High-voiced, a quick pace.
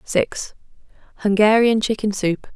No: high, 210 Hz; slow, 70 wpm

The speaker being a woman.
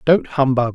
No: male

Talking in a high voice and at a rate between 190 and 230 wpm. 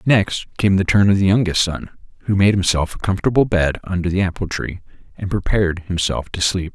No: very low, 95 Hz; fast, 205 wpm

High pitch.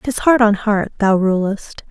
Yes: high, 210 Hz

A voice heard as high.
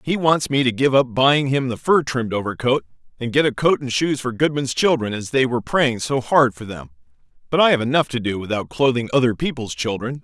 No: low, 130 Hz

